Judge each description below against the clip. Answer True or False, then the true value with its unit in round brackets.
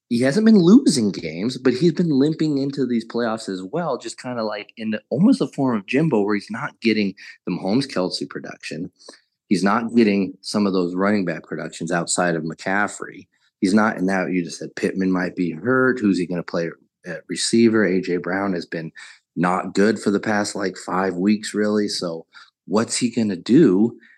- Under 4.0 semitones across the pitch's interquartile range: False (4.6 semitones)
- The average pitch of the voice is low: True (105 Hz)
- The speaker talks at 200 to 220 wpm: True (205 wpm)